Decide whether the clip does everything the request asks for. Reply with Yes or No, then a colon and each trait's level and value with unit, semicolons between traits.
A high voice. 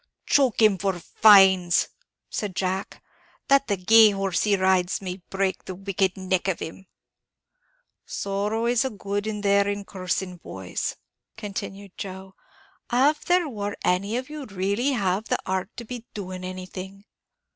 Yes: high, 195 Hz